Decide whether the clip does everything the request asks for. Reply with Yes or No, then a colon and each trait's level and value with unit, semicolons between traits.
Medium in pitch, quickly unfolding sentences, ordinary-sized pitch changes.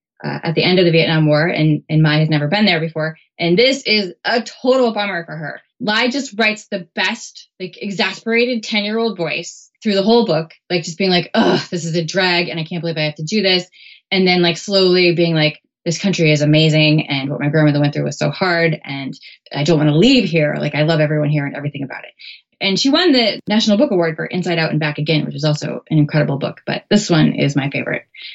Yes: medium, 170 Hz; fast, 250 wpm; average, 4.7 semitones